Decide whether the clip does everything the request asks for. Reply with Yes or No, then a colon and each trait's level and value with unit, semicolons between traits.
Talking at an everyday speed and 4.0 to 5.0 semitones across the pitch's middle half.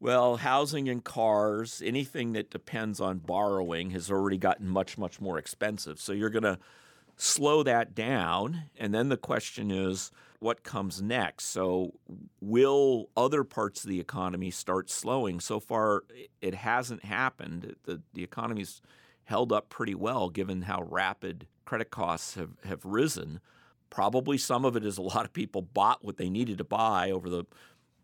Yes: average, 165 wpm; average, 4.3 semitones